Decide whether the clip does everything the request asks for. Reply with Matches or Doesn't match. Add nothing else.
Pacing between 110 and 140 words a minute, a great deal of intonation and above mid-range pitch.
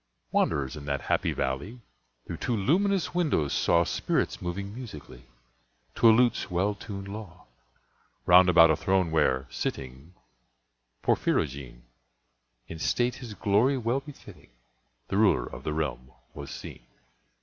Doesn't match